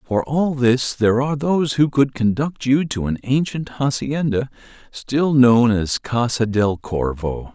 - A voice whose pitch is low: Yes, low, 125 Hz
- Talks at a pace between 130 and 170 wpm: Yes, average, 150 wpm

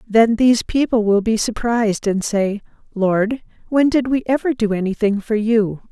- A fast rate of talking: No, average, 175 wpm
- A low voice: No, high, 220 Hz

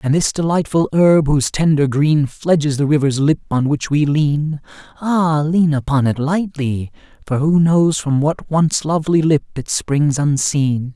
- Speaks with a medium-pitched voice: Yes, medium, 150 Hz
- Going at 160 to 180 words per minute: Yes, average, 170 wpm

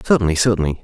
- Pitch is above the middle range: No, very low, 95 Hz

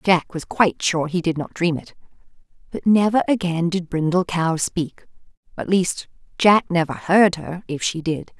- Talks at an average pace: Yes, average, 170 wpm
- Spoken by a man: No, female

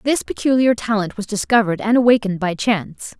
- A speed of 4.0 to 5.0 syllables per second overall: No, 6.2 syllables/s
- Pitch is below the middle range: No, high, 215 Hz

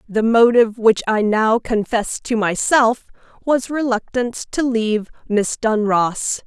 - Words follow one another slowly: Yes, slow, 130 wpm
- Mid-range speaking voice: No, high, 225 Hz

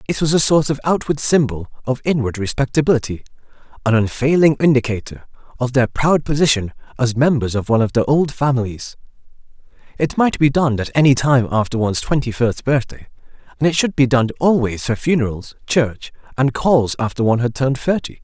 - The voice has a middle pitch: No, low, 130 Hz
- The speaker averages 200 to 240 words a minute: No, average, 170 wpm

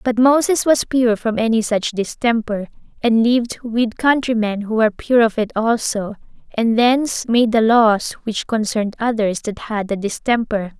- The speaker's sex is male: No, female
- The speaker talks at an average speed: Yes, average, 165 wpm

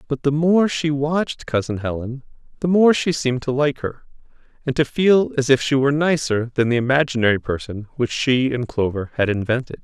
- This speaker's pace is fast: No, average, 195 wpm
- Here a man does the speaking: Yes, male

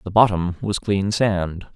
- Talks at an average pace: Yes, average, 170 wpm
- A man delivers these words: Yes, male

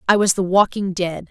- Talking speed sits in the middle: No, fast, 230 wpm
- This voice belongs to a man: No, female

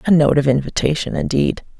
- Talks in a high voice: No, medium, 155 Hz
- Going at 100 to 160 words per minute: No, average, 170 wpm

